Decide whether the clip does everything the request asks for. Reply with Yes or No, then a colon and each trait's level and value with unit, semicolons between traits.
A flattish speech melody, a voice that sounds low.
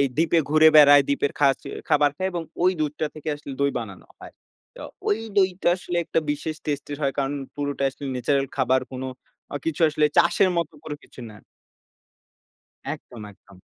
No: narrow, 2.3 semitones; medium, 145 Hz